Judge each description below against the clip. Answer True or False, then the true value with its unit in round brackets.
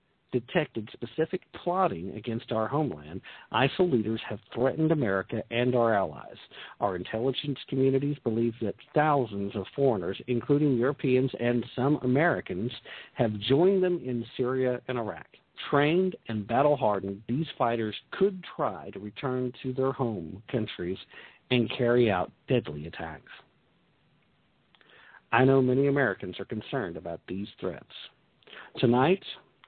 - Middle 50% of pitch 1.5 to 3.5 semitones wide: False (4.0 semitones)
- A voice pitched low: True (125 Hz)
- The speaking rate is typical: False (125 wpm)